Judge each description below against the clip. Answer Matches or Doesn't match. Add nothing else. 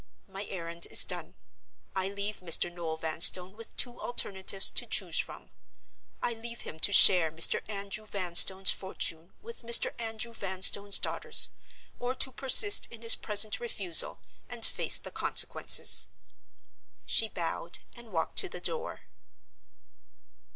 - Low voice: Doesn't match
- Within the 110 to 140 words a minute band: Matches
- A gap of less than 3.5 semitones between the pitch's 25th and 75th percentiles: Doesn't match